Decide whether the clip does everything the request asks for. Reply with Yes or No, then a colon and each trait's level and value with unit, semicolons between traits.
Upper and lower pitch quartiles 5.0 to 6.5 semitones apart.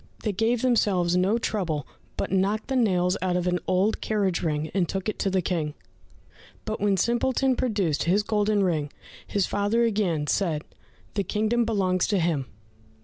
No: average, 3.4 semitones